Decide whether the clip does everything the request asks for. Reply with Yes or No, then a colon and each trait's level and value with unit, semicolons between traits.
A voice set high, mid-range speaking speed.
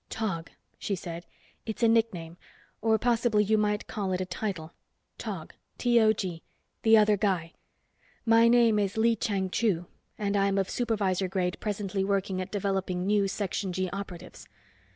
Yes: high, 200 Hz; average, 160 wpm